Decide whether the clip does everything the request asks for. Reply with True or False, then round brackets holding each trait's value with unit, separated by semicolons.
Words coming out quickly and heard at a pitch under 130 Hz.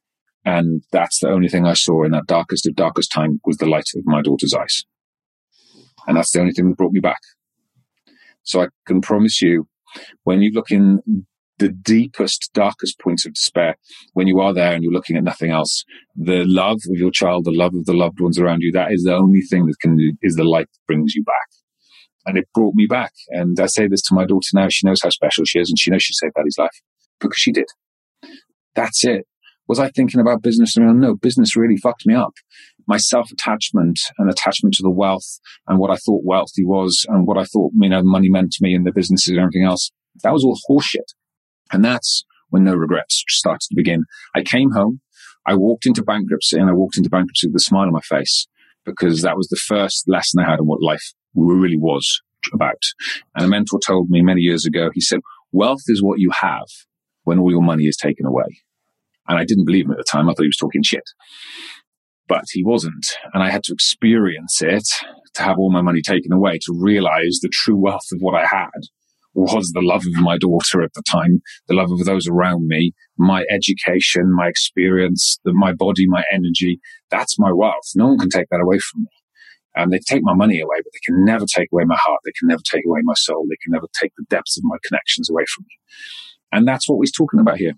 True (230 wpm; 90 Hz)